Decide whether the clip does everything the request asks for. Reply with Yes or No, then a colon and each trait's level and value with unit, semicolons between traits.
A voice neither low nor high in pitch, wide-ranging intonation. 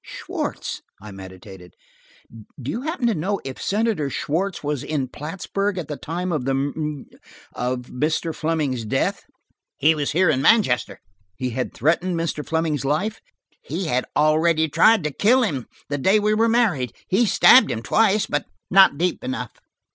Yes: medium, 155 Hz; wide, 6.4 semitones